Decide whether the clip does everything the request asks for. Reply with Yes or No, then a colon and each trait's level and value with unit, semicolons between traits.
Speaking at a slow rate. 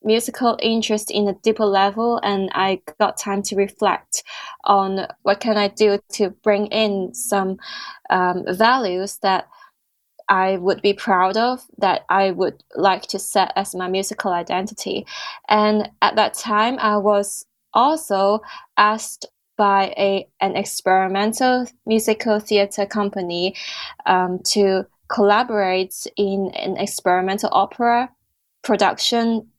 Yes: slow, 125 wpm